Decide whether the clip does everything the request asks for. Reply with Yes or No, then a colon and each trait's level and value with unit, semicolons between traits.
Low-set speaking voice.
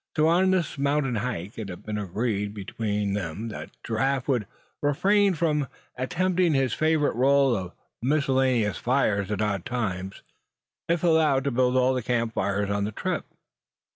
Yes: low, 125 Hz